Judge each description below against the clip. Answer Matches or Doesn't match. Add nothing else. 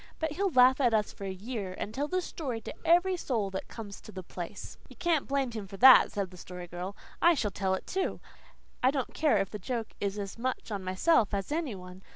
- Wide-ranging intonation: Matches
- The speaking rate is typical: Doesn't match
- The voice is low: Doesn't match